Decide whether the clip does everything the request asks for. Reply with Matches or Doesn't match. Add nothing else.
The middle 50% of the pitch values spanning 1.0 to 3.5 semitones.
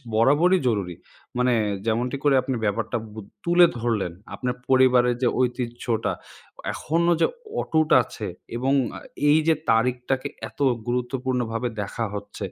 Matches